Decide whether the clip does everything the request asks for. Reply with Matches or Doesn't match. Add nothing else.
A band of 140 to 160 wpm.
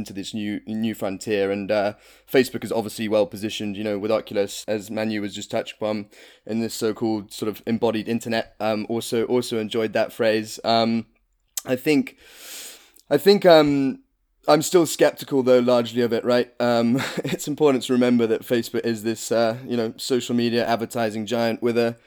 Doesn't match